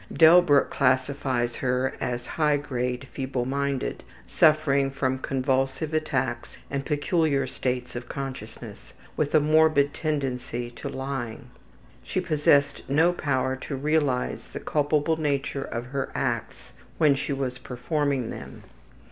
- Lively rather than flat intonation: No, narrow, 2.5 semitones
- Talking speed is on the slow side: Yes, slow, 120 wpm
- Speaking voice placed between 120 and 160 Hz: Yes, medium, 140 Hz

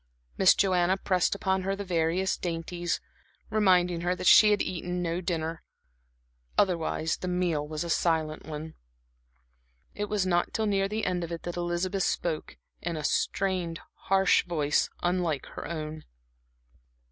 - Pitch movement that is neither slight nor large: No, narrow, 2.3 semitones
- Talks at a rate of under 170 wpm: Yes, average, 150 wpm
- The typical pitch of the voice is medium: Yes, medium, 175 Hz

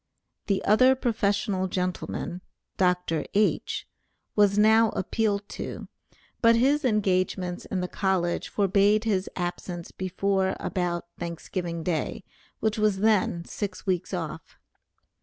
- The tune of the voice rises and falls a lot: No, average, 2.9 semitones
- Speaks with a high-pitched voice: Yes, high, 195 Hz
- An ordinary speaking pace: No, slow, 115 wpm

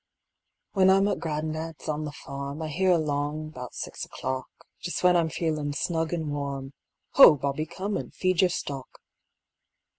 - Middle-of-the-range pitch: Yes, medium, 155 Hz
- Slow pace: No, average, 160 wpm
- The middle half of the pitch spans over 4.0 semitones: No, average, 3.2 semitones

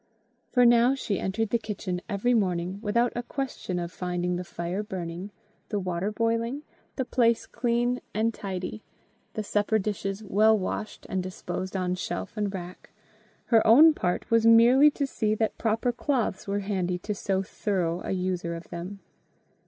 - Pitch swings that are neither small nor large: Yes, average, 3.8 semitones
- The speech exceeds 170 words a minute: No, average, 165 wpm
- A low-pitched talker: No, high, 205 Hz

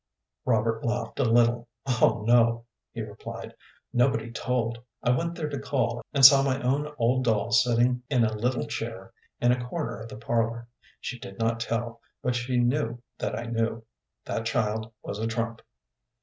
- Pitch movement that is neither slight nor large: No, narrow, 1.6 semitones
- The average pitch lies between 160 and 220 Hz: No, low, 120 Hz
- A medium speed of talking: Yes, average, 175 wpm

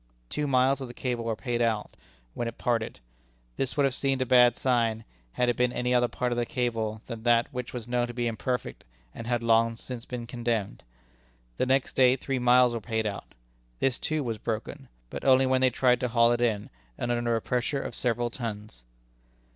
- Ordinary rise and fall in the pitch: No, narrow, 1.6 semitones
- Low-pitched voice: Yes, low, 120 Hz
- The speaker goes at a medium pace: No, fast, 210 wpm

